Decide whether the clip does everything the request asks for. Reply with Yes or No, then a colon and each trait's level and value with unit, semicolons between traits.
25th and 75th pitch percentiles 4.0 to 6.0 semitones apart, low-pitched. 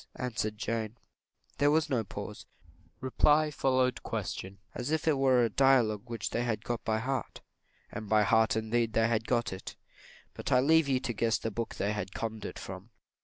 No: average, 3.2 semitones; low, 115 Hz